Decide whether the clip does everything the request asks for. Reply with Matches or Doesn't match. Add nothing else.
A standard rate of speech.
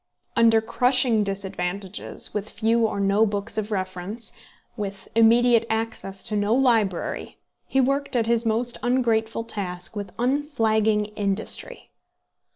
Doesn't match